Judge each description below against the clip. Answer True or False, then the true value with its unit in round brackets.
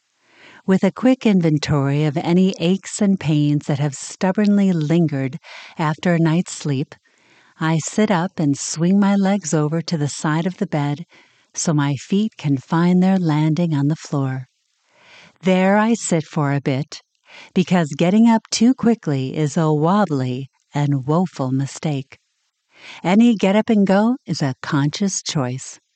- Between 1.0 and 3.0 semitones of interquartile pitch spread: False (4.8 semitones)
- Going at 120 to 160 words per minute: True (155 wpm)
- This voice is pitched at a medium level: True (165 Hz)